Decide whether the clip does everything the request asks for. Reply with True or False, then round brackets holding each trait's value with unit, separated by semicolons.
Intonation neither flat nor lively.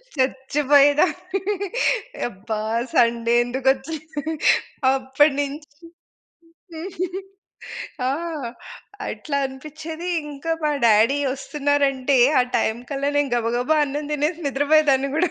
False (2.3 semitones)